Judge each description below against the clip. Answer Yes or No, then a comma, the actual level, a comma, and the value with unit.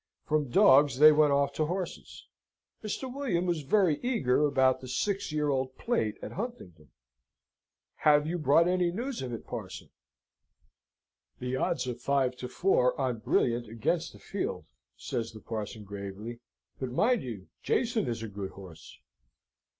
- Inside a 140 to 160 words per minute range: Yes, average, 155 wpm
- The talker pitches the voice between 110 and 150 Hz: Yes, low, 135 Hz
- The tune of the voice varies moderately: No, wide, 6.6 semitones